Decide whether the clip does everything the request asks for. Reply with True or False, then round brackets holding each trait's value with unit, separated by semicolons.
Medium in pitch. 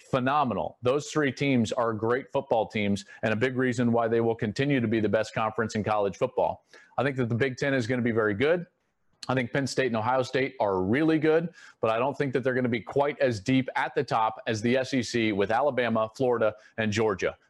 False (125 Hz)